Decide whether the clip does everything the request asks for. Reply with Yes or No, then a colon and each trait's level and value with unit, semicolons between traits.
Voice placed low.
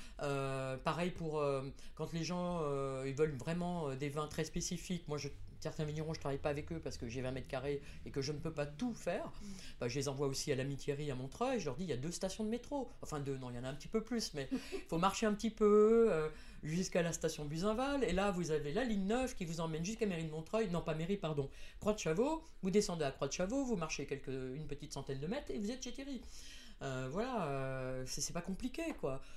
No: medium, 160 Hz